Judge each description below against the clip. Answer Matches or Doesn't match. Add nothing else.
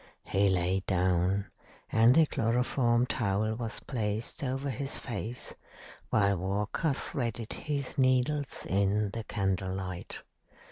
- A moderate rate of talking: Doesn't match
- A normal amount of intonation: Matches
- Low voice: Matches